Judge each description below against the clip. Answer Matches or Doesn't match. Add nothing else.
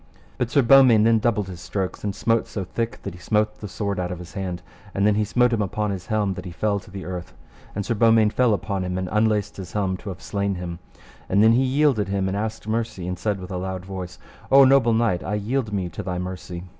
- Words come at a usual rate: Doesn't match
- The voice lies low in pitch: Matches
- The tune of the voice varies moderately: Matches